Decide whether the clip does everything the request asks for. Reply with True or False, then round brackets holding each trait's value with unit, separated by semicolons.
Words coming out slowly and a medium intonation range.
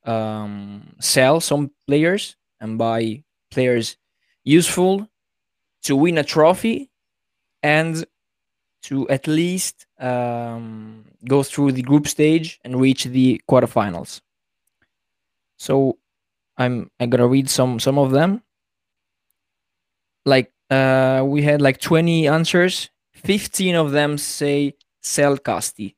True (110 wpm; 4.7 semitones)